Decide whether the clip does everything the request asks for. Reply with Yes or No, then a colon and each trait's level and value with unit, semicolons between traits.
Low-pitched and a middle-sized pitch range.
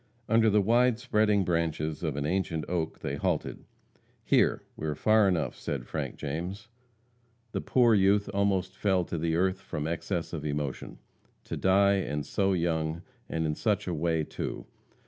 Yes: very low, 90 Hz; average, 4.0 semitones